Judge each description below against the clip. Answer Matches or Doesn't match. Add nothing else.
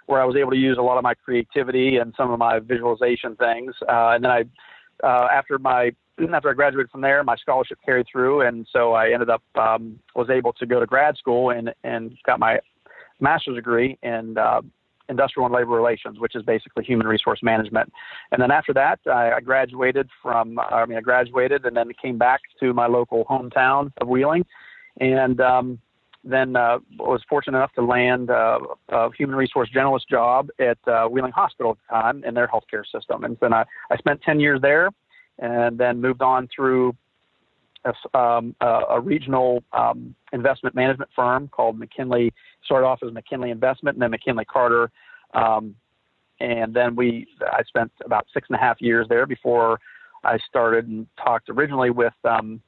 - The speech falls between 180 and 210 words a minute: Matches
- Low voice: Matches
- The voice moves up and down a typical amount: Doesn't match